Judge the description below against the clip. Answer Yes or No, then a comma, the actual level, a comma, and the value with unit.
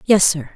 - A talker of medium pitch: Yes, medium, 180 Hz